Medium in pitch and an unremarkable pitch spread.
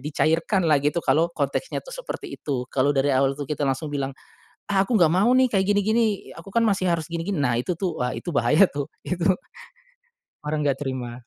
No: medium, 155 Hz; wide, 5.7 semitones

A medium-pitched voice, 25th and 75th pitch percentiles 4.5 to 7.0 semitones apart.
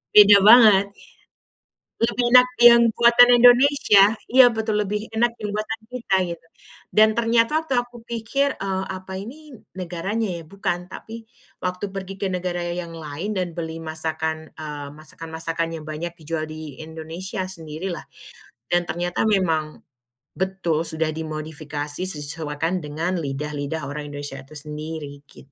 Yes: medium, 175 Hz; average, 5.3 semitones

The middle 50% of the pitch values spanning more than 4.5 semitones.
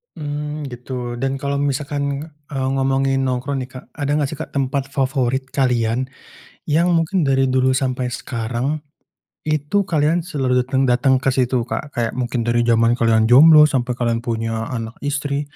No: average, 2.7 semitones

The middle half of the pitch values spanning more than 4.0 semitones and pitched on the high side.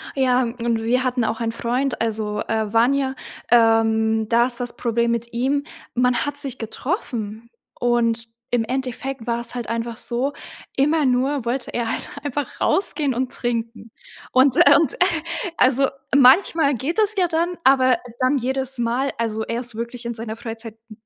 No: narrow, 2.6 semitones; high, 245 Hz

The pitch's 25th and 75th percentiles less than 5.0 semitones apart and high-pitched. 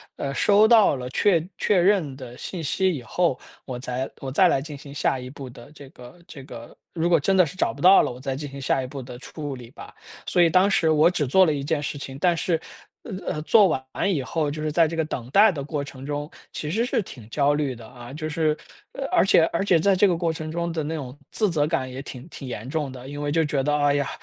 No: average, 4.1 semitones; medium, 150 Hz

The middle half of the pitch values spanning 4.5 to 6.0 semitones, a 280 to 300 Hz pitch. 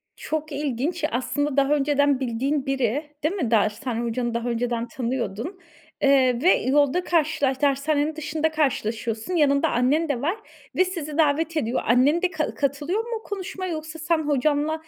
No: average, 3.8 semitones; very high, 285 Hz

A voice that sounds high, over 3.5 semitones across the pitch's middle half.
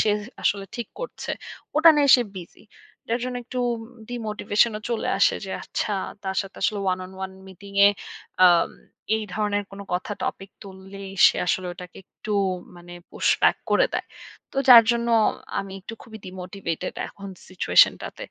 No: high, 200 Hz; average, 3.2 semitones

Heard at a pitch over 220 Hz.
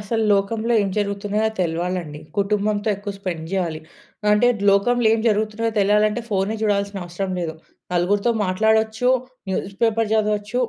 No: high, 205 Hz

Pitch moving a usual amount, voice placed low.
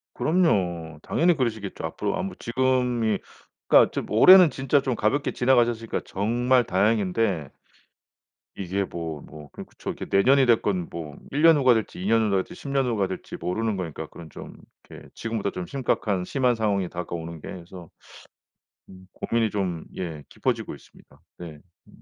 No: wide, 5.9 semitones; low, 105 Hz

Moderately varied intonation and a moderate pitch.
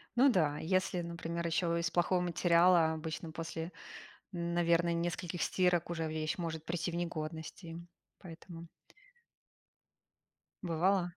No: narrow, 1.3 semitones; medium, 170 Hz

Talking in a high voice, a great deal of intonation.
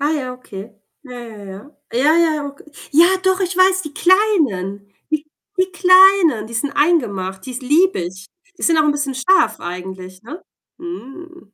Yes: very high, 285 Hz; wide, 8.6 semitones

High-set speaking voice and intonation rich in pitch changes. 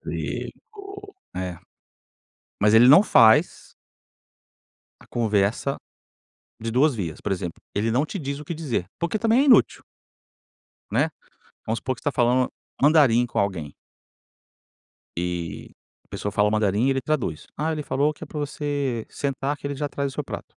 No: low, 130 Hz; wide, 5.9 semitones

